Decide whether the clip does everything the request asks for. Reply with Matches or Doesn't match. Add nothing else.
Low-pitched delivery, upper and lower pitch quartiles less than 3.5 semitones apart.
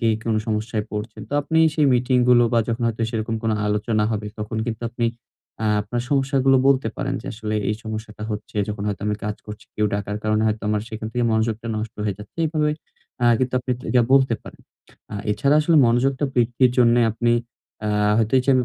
Matches